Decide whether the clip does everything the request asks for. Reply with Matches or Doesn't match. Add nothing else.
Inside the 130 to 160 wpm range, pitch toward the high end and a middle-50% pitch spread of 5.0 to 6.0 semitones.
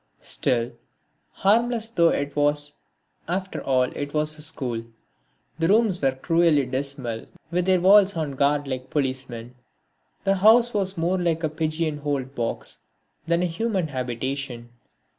Doesn't match